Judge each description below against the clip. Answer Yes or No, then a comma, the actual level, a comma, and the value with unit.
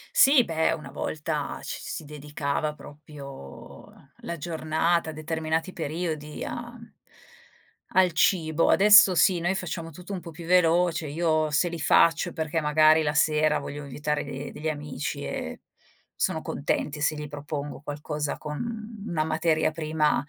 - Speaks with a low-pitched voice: No, medium, 155 Hz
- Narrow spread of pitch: Yes, narrow, 2.2 semitones